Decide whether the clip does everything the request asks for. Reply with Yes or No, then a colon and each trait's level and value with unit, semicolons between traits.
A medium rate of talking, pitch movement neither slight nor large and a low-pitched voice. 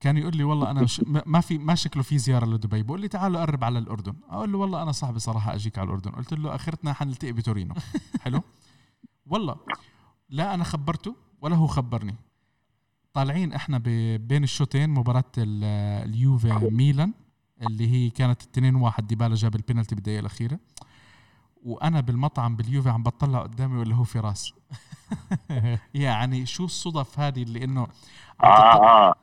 No: fast, 155 wpm; average, 4.3 semitones; low, 125 Hz